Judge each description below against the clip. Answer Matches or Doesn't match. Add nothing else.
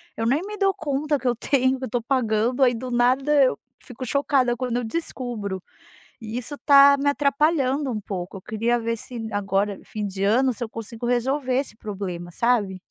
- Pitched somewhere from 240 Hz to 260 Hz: Matches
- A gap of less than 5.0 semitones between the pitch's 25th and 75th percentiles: Matches